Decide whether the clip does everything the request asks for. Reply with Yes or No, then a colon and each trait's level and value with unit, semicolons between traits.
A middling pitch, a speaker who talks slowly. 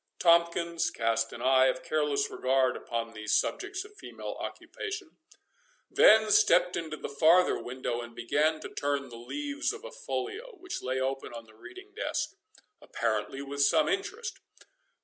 No: medium, 155 Hz; average, 155 wpm